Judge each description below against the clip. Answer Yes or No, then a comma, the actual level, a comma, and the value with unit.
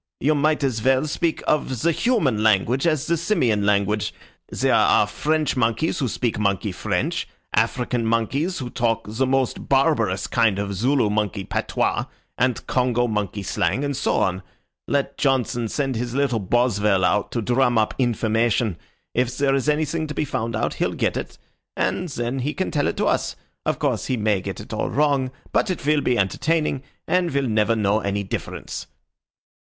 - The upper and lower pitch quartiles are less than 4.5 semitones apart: No, average, 4.8 semitones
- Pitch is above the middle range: No, low, 125 Hz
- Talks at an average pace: Yes, average, 180 wpm